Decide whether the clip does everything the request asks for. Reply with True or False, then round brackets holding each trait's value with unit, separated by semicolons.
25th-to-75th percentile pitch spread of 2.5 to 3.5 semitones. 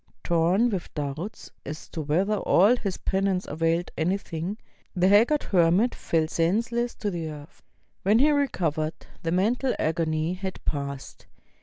False (4.5 semitones)